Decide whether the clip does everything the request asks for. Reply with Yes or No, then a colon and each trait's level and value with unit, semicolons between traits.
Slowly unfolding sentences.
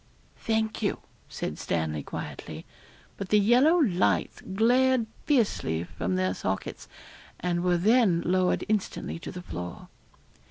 Yes: slow, 125 wpm